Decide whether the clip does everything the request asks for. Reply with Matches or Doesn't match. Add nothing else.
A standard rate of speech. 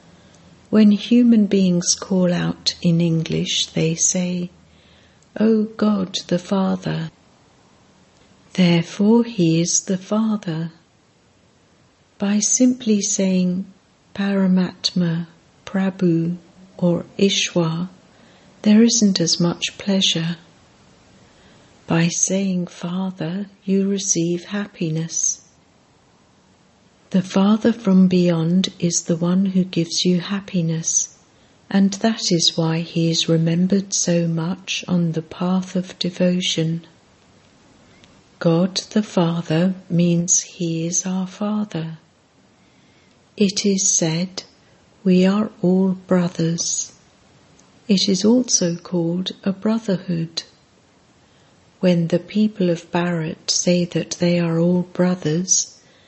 Doesn't match